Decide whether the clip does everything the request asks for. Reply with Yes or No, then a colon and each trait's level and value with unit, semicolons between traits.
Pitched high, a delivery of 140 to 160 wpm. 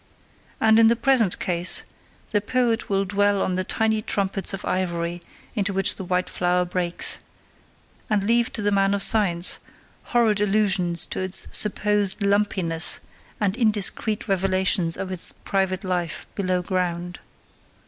Yes: high, 195 Hz; average, 145 wpm